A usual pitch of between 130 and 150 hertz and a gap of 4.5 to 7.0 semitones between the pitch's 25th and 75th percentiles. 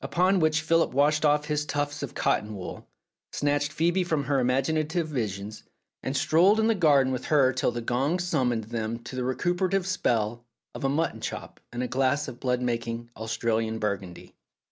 Yes: low, 135 Hz; average, 4.9 semitones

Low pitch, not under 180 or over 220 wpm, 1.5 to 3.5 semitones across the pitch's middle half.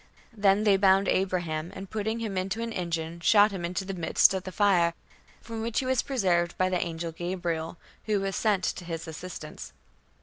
No: medium, 185 Hz; average, 195 wpm; average, 3.0 semitones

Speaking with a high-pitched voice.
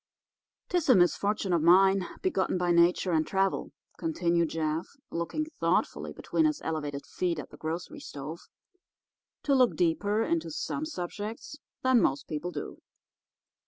No: medium, 180 Hz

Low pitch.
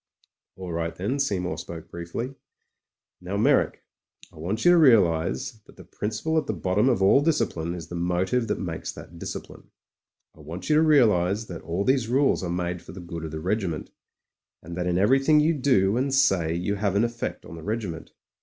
Yes: very low, 95 Hz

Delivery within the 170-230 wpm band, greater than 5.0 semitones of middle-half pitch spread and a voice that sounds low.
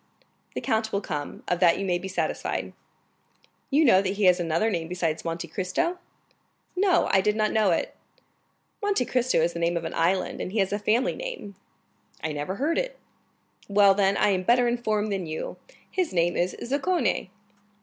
No: average, 190 wpm; wide, 5.5 semitones; high, 195 Hz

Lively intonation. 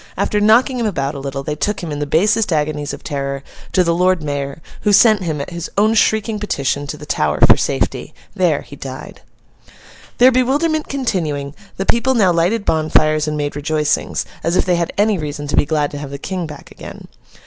Yes: wide, 6.2 semitones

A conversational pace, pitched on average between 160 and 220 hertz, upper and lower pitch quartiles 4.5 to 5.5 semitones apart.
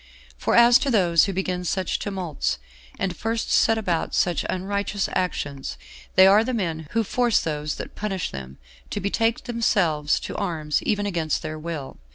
Yes: average, 170 wpm; medium, 185 Hz; average, 4.9 semitones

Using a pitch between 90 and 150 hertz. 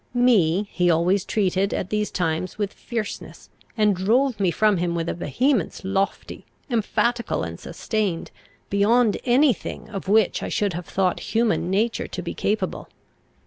No: high, 200 Hz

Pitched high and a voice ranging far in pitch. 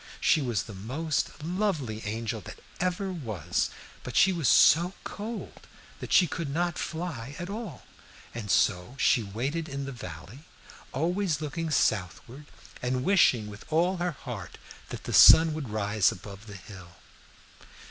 No: medium, 140 Hz; wide, 7.8 semitones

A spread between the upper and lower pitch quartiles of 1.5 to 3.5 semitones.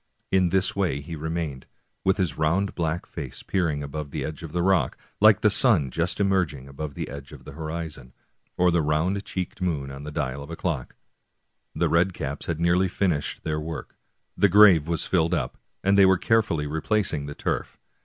No: average, 4.1 semitones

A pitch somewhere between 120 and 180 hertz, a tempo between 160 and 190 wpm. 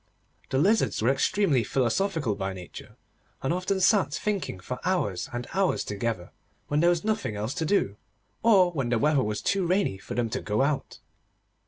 Yes: medium, 140 Hz; average, 180 wpm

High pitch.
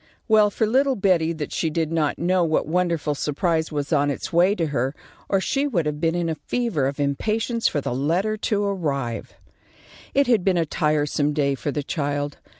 No: medium, 165 Hz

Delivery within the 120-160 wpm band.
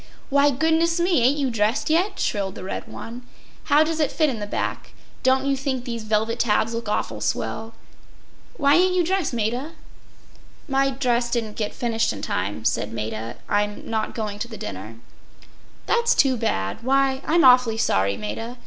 No: average, 175 wpm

